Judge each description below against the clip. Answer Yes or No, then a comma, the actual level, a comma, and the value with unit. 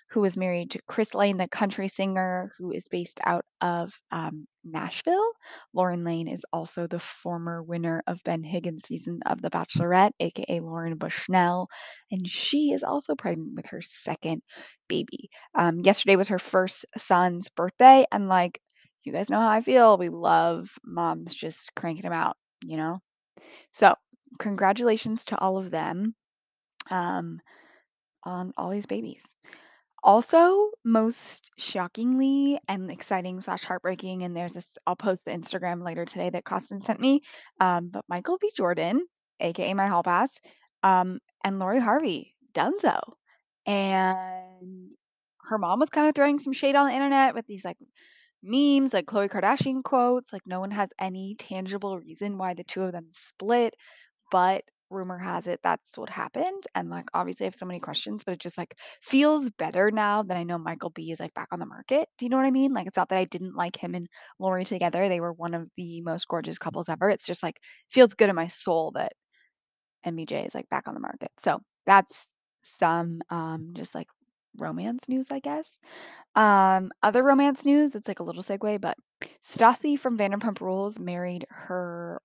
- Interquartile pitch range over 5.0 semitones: Yes, wide, 5.5 semitones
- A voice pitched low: No, high, 190 Hz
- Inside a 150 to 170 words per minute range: No, average, 180 wpm